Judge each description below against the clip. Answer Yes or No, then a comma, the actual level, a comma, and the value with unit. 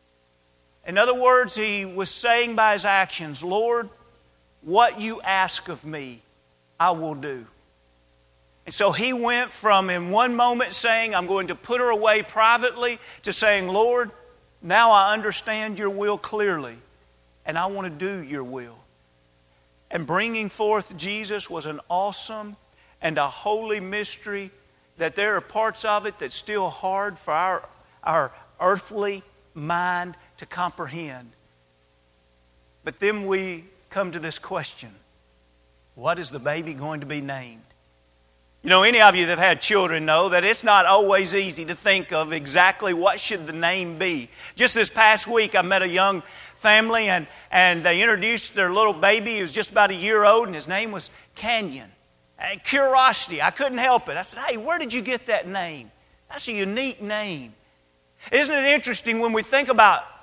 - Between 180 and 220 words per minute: No, average, 170 wpm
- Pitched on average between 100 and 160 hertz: No, high, 190 Hz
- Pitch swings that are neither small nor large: No, wide, 6.0 semitones